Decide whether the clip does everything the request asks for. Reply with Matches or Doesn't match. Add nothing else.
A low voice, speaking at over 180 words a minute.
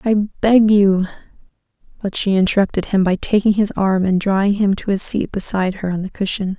Doesn't match